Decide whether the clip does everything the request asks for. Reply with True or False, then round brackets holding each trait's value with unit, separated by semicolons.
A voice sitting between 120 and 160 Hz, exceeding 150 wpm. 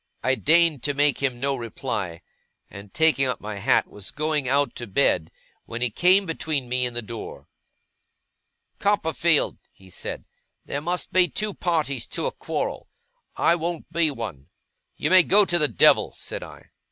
True (140 Hz; 170 wpm)